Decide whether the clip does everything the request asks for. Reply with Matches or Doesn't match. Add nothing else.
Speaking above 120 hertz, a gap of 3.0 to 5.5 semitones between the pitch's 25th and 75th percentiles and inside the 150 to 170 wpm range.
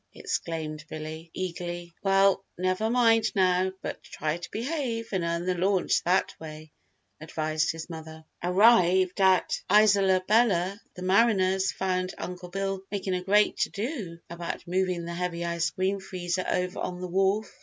Doesn't match